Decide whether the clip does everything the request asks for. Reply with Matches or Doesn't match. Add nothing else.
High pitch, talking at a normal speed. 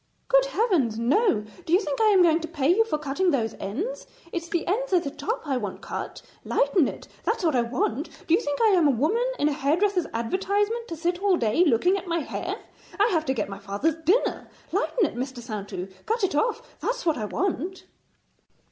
Doesn't match